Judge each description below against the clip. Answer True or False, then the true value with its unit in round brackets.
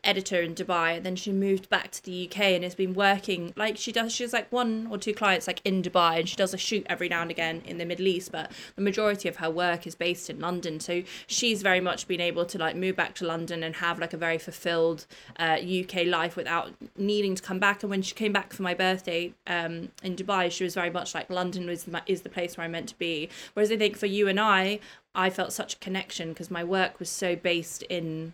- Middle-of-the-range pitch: True (180 Hz)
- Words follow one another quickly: True (260 wpm)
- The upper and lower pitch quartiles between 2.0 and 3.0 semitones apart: True (2.5 semitones)